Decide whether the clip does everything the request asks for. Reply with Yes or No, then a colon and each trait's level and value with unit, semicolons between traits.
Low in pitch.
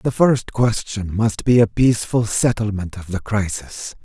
Yes: low, 110 Hz